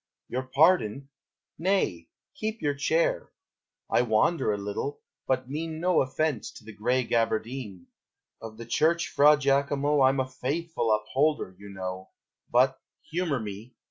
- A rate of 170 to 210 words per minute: No, average, 140 wpm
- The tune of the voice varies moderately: No, wide, 5.8 semitones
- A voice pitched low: Yes, low, 130 Hz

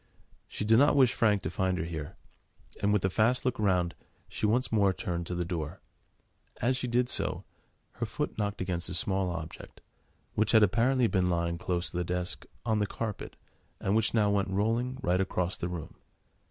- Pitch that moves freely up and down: No, average, 4.2 semitones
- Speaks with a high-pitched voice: No, low, 100 Hz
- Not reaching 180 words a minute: No, average, 195 wpm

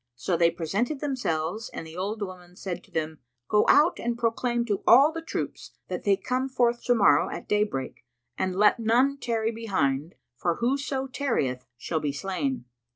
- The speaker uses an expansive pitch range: Yes, wide, 6.3 semitones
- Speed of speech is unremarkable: Yes, average, 175 wpm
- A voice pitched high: Yes, high, 210 Hz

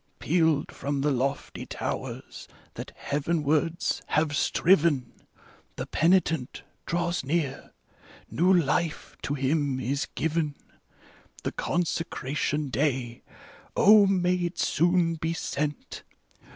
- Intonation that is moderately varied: Yes, average, 3.4 semitones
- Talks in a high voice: No, medium, 155 Hz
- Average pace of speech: No, slow, 105 wpm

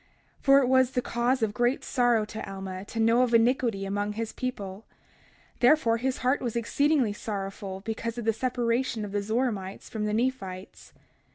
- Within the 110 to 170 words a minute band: No, average, 180 wpm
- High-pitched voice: Yes, high, 230 Hz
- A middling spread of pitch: Yes, average, 3.5 semitones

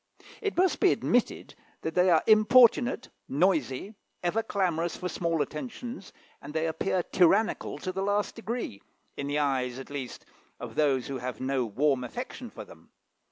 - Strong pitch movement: Yes, wide, 7.2 semitones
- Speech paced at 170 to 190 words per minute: No, average, 160 wpm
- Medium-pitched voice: Yes, medium, 170 Hz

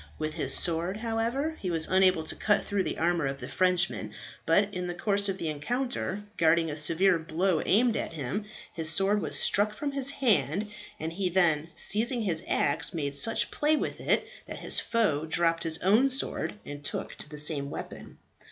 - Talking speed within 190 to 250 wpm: Yes, average, 195 wpm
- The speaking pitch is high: No, medium, 180 Hz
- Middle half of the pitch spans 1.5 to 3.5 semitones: No, average, 4.8 semitones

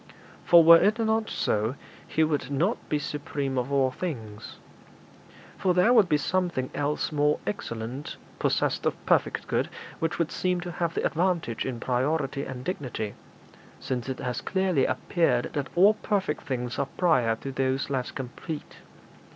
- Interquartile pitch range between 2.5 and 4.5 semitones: No, average, 5.1 semitones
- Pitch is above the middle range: No, medium, 145 Hz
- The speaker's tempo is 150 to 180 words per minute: Yes, average, 160 wpm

